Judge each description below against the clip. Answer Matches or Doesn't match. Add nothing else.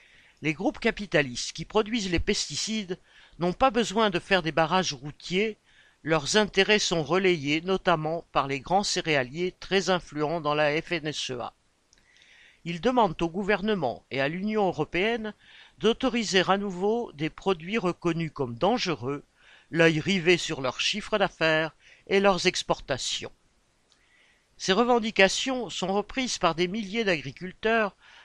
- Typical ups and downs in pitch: Matches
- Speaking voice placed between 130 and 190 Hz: Matches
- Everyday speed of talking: Doesn't match